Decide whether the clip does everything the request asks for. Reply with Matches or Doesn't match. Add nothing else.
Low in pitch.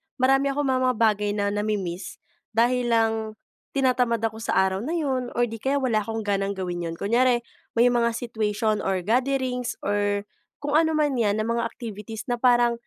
Doesn't match